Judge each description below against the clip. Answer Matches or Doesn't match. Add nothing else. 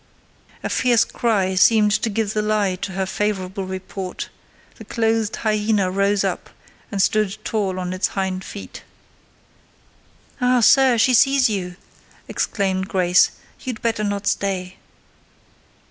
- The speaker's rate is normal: Doesn't match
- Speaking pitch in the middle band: Doesn't match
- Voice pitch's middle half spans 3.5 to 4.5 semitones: Doesn't match